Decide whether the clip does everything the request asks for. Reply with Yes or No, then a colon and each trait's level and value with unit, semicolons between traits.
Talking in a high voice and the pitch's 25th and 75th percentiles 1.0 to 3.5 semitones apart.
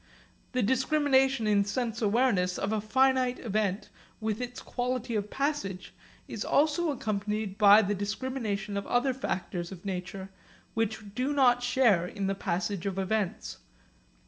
No: high, 215 Hz; average, 4.3 semitones